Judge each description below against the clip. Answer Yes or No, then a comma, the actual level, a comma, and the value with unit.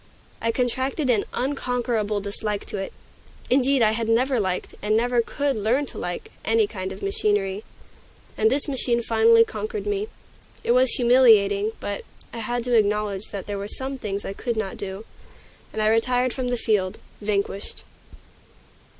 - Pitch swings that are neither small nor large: Yes, average, 3.7 semitones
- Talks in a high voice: Yes, high, 225 Hz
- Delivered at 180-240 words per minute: No, average, 165 wpm